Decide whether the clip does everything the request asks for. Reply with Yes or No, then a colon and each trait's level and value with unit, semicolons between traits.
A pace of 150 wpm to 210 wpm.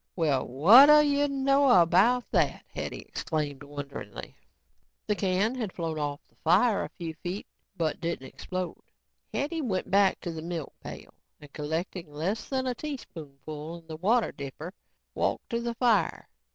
Yes: average, 160 wpm